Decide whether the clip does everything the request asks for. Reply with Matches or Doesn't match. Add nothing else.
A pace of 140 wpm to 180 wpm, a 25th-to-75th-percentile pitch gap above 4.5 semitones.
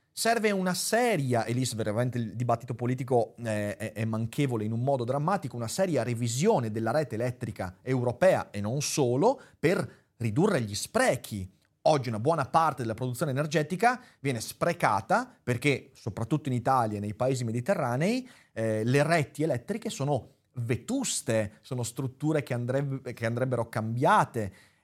Matches